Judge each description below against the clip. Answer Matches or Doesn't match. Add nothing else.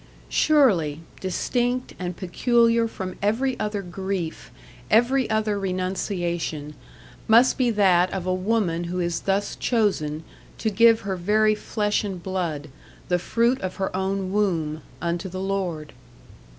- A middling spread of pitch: Matches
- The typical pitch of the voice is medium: Doesn't match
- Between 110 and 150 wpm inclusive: Matches